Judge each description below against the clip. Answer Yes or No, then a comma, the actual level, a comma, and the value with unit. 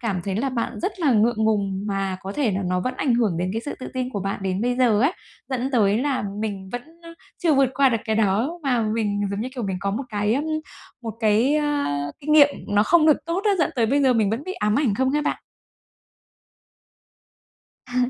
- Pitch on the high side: Yes, high, 235 Hz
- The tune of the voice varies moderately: Yes, average, 5.0 semitones